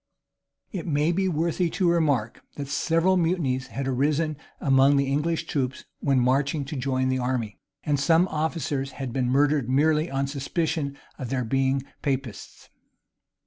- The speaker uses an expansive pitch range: No, average, 3.2 semitones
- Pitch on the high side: No, medium, 140 Hz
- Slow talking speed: No, average, 155 wpm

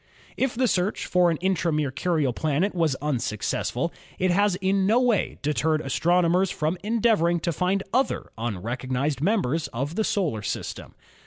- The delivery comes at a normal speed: Yes, average, 160 wpm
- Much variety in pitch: No, average, 5.0 semitones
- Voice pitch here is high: No, medium, 170 Hz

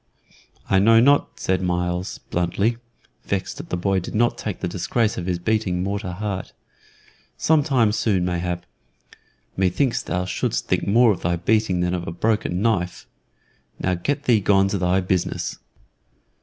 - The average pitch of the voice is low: Yes, very low, 95 Hz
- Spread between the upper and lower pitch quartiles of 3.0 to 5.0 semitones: Yes, average, 3.7 semitones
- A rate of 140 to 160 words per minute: No, average, 170 wpm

